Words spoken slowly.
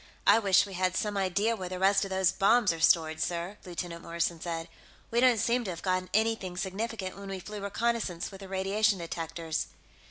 No: average, 200 wpm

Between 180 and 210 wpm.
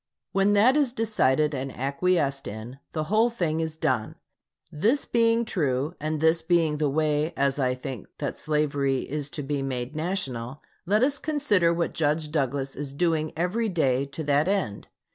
No: average, 170 wpm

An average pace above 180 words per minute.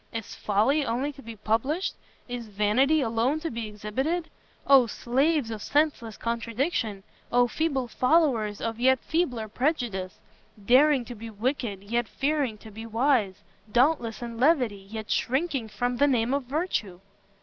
No: average, 150 wpm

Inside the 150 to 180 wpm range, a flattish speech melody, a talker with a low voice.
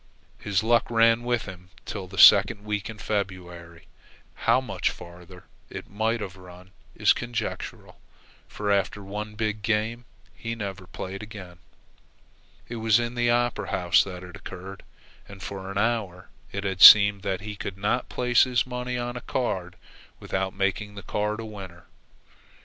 No: average, 160 wpm; average, 3.2 semitones; low, 100 Hz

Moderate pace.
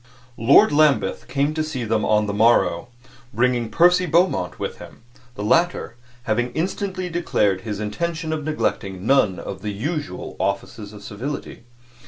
Yes: average, 150 wpm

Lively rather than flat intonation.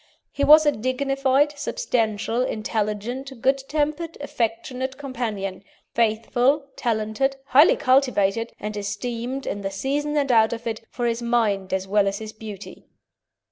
No: average, 4.2 semitones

